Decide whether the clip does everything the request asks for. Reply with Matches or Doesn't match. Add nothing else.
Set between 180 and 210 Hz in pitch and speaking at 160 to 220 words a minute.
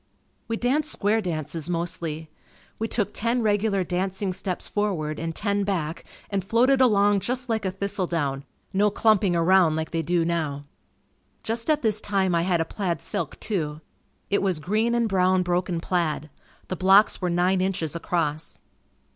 Matches